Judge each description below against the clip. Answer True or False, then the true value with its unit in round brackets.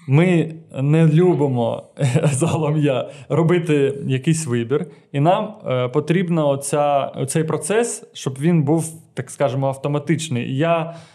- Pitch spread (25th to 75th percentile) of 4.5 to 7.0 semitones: False (2.8 semitones)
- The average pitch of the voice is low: False (155 Hz)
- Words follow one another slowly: True (95 wpm)